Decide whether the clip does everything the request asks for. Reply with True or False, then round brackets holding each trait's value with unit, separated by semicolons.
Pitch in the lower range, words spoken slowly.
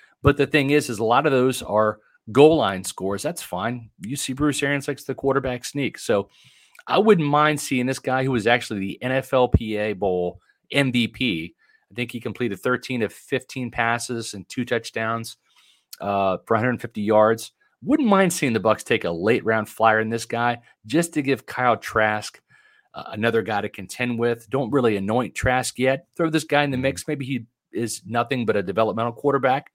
False (120 Hz; 190 wpm)